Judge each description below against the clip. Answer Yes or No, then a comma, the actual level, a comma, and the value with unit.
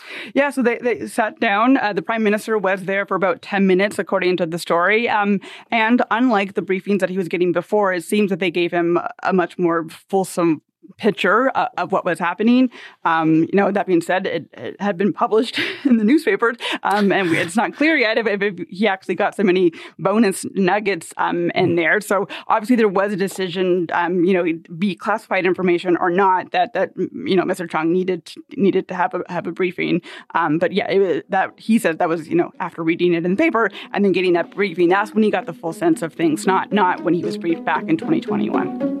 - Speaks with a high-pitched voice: Yes, high, 195 Hz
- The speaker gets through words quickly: Yes, fast, 225 wpm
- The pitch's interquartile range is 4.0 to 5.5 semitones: No, average, 3.5 semitones